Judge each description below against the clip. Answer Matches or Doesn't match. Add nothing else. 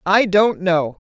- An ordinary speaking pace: Matches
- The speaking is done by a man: Doesn't match